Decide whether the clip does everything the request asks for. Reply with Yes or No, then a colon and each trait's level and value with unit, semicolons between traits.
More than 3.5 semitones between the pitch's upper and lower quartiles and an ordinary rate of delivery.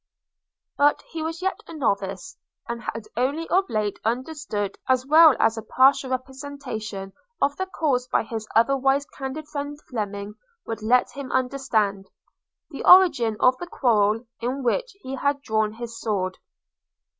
Yes: average, 4.6 semitones; average, 150 wpm